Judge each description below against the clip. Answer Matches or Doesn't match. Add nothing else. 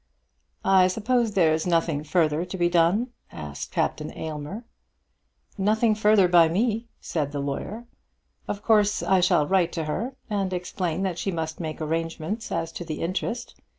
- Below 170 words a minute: Matches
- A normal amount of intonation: Matches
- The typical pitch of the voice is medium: Matches